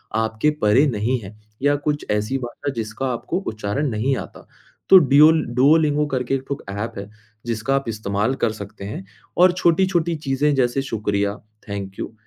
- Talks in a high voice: No, low, 125 Hz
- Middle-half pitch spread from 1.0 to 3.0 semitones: No, average, 5.2 semitones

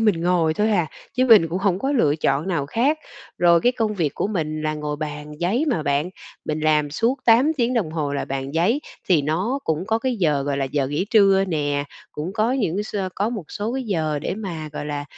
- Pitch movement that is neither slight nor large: No, wide, 6.3 semitones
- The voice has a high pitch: No, medium, 175 Hz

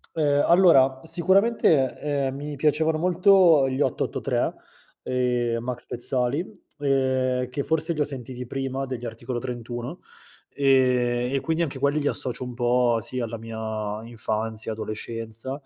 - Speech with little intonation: No, average, 3.3 semitones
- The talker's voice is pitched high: No, low, 130 Hz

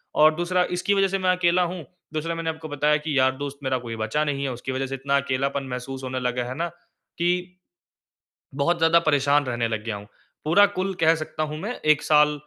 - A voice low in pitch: No, medium, 150 Hz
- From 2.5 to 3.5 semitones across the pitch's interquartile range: No, average, 4.3 semitones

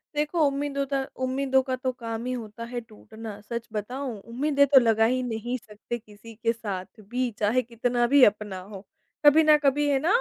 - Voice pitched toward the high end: Yes, high, 245 Hz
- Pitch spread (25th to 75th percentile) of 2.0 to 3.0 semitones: No, average, 3.6 semitones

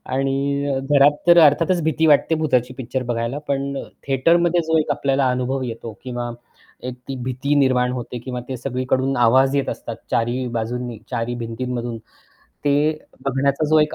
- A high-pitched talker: No, low, 130 Hz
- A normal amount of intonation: No, narrow, 2.3 semitones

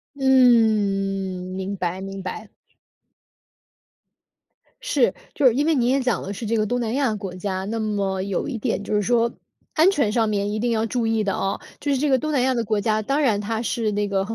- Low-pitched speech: No, high, 220 Hz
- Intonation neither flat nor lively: Yes, average, 3.8 semitones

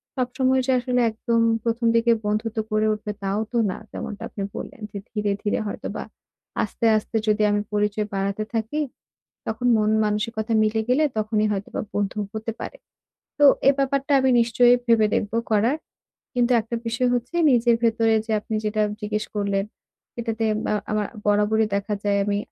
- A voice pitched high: Yes, high, 220 Hz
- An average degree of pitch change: No, narrow, 2.2 semitones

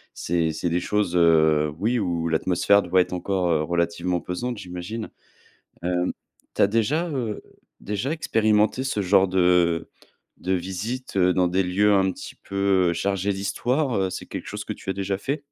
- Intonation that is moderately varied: Yes, average, 3.0 semitones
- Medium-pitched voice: No, very low, 95 Hz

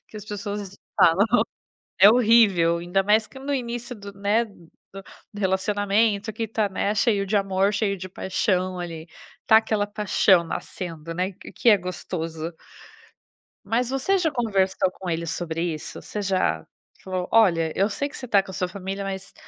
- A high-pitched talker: Yes, high, 200 Hz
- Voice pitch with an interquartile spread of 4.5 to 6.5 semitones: No, average, 3.0 semitones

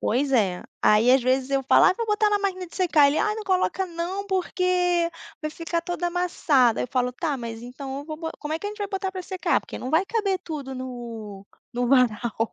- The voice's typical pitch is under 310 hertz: No, very high, 315 Hz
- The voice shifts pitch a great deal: Yes, wide, 6.6 semitones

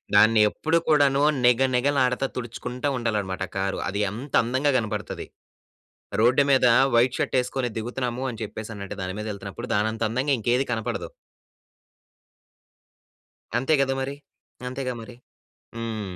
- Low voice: Yes, low, 120 Hz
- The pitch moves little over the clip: No, average, 3.3 semitones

